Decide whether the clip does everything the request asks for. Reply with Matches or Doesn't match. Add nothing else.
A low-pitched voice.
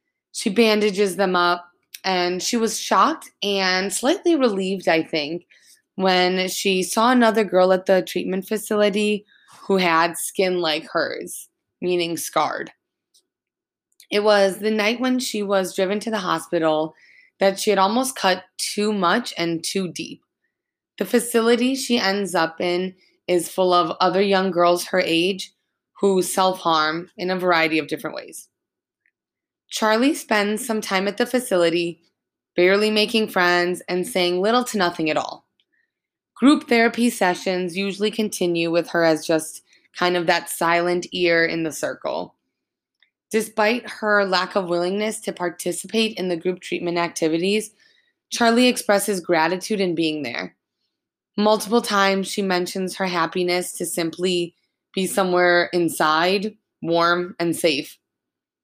Doesn't match